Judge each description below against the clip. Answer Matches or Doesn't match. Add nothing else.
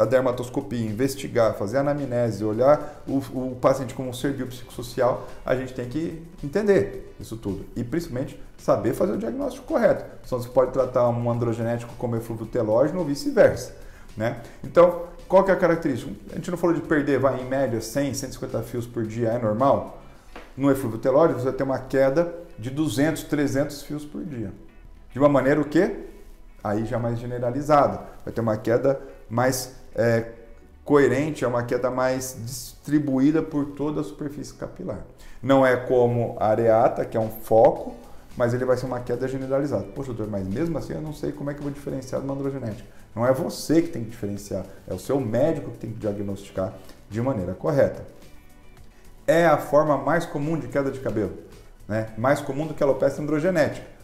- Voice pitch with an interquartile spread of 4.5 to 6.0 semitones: Doesn't match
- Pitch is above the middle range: Doesn't match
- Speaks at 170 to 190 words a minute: Matches